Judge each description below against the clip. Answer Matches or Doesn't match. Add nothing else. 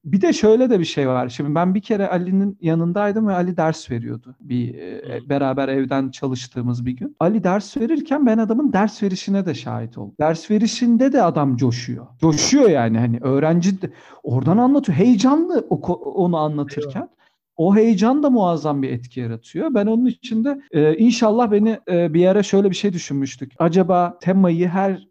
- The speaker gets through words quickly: Matches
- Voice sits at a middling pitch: Matches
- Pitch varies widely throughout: Matches